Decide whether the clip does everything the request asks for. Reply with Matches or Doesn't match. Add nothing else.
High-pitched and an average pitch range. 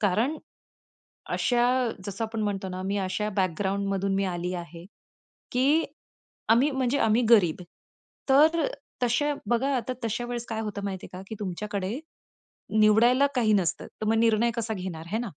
Matches